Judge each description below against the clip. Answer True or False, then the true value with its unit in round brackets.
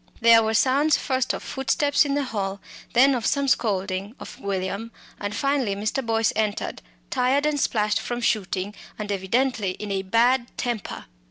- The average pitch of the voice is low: False (225 Hz)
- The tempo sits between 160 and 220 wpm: True (165 wpm)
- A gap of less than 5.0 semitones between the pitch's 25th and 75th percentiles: True (4.5 semitones)